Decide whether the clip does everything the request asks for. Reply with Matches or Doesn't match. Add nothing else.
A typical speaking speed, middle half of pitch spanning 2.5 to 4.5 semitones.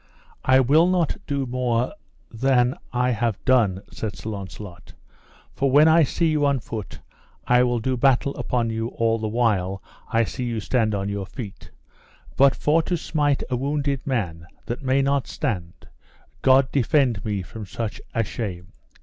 Matches